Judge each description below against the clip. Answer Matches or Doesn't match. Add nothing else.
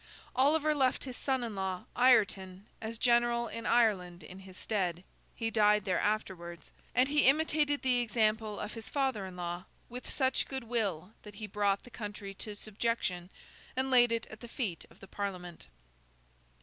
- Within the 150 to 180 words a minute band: Matches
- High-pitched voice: Matches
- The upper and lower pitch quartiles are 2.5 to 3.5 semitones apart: Doesn't match